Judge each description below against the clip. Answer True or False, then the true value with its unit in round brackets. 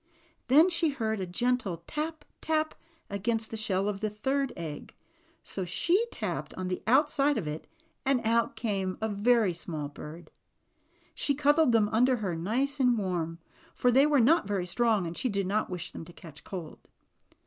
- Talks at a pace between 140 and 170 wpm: False (180 wpm)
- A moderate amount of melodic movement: False (6.6 semitones)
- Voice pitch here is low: False (220 Hz)